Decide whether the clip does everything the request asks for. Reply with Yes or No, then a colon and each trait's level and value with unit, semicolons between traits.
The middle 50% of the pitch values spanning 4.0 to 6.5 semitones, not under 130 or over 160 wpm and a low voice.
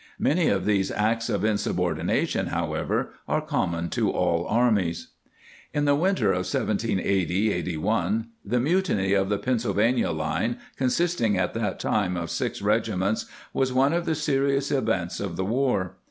Yes: wide, 5.5 semitones; average, 155 wpm; low, 105 Hz